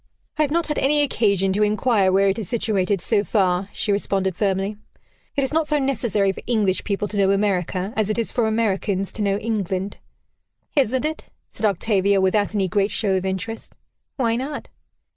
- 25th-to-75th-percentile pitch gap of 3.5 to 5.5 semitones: No, average, 3.1 semitones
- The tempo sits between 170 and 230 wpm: Yes, average, 190 wpm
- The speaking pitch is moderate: No, high, 205 Hz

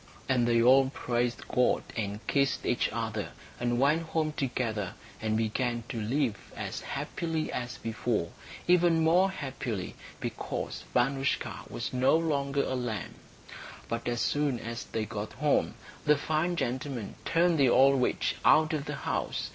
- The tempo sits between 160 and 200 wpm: No, average, 150 wpm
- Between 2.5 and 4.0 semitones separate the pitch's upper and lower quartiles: No, average, 4.4 semitones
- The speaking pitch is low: Yes, low, 130 Hz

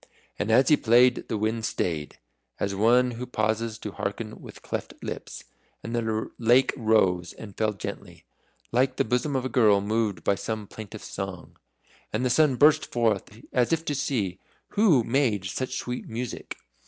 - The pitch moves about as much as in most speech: Yes, average, 3.1 semitones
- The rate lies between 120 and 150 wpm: No, average, 170 wpm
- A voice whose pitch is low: Yes, low, 115 Hz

